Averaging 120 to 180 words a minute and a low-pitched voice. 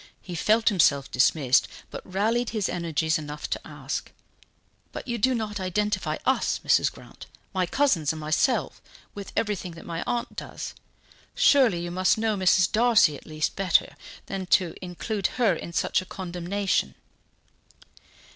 No: average, 150 wpm; medium, 185 Hz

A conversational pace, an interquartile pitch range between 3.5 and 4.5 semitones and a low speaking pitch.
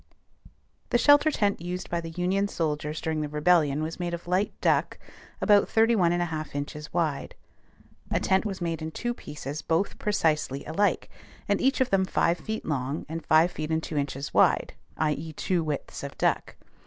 No: average, 180 wpm; average, 3.8 semitones; medium, 165 Hz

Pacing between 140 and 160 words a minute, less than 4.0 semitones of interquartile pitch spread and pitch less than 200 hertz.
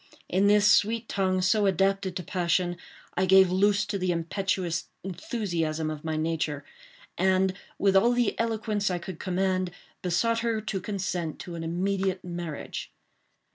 Yes: average, 150 wpm; narrow, 2.6 semitones; high, 190 Hz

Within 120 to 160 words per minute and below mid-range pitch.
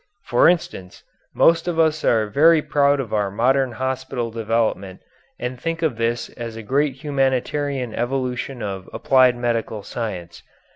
Yes: average, 145 wpm; low, 125 Hz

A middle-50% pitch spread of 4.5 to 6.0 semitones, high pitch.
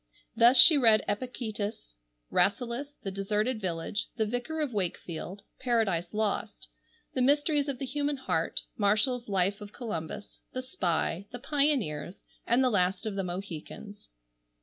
Yes: average, 4.8 semitones; high, 215 Hz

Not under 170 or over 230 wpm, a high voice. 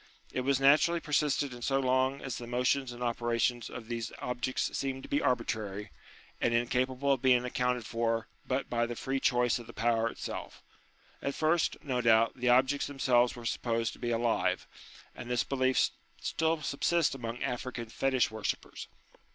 No: average, 175 wpm; low, 125 Hz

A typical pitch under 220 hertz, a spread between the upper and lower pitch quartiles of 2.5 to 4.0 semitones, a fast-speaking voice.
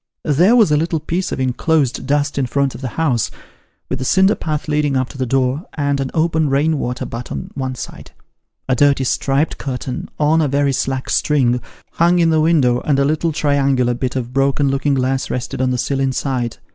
Yes: medium, 140 Hz; average, 2.9 semitones; fast, 210 wpm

